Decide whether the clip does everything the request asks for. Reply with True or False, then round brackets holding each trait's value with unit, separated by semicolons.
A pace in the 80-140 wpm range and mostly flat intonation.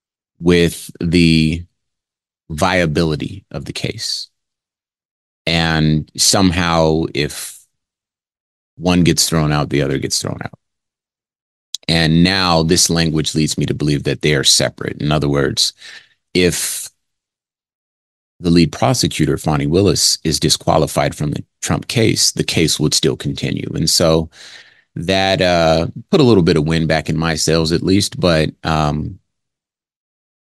True (135 wpm; 2.0 semitones)